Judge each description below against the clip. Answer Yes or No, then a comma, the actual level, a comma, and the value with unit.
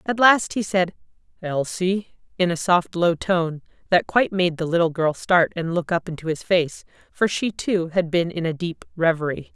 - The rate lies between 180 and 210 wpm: Yes, average, 200 wpm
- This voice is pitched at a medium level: Yes, medium, 175 Hz